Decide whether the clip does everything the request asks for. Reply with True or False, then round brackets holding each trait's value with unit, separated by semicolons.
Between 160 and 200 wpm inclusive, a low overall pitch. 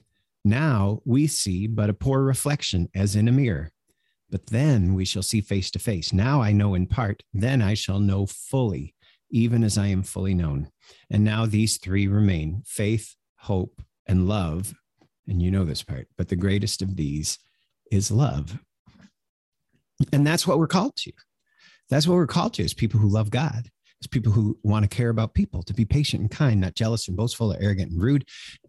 True (195 wpm; 105 Hz)